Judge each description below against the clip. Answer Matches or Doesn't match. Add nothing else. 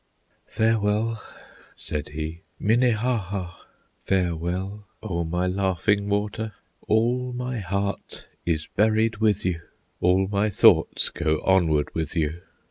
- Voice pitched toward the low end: Matches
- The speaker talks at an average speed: Doesn't match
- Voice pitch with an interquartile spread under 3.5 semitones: Doesn't match